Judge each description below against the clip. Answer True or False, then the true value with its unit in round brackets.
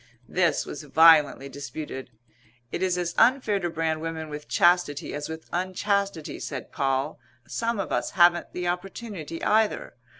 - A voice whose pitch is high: False (170 Hz)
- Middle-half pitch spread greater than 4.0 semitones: False (3.7 semitones)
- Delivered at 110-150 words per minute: True (145 wpm)